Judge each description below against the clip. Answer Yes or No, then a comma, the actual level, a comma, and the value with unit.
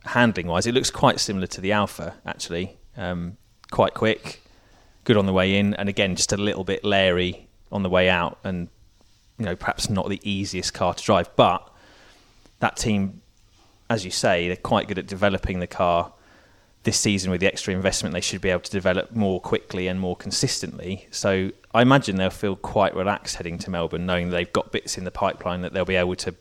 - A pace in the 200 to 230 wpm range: Yes, fast, 205 wpm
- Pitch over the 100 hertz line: No, very low, 95 Hz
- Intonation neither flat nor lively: No, narrow, 2.1 semitones